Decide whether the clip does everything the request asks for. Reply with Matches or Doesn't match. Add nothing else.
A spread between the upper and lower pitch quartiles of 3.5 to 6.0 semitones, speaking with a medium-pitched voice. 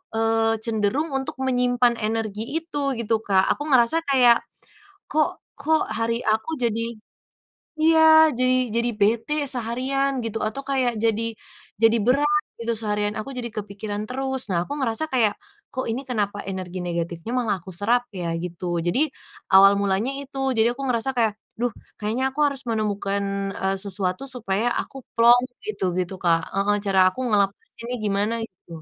Doesn't match